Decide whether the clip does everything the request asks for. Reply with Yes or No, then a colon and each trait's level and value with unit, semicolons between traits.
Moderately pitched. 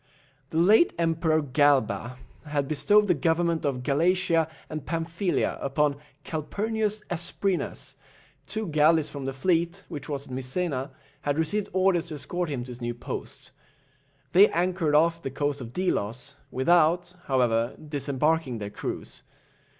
Yes: medium, 155 Hz